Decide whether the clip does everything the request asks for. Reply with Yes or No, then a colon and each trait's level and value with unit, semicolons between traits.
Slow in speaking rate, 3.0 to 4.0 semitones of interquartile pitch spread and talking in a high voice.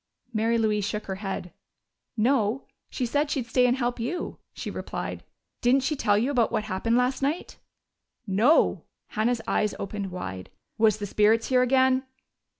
No: average, 160 wpm; average, 3.7 semitones; high, 230 Hz